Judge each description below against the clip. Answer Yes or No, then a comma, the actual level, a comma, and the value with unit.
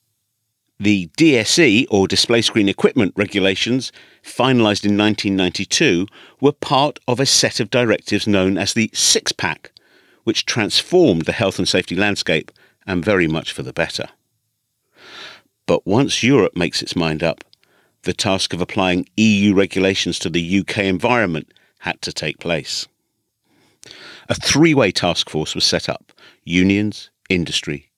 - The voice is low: Yes, low, 100 Hz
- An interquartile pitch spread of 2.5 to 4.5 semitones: Yes, average, 2.8 semitones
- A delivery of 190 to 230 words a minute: No, slow, 135 wpm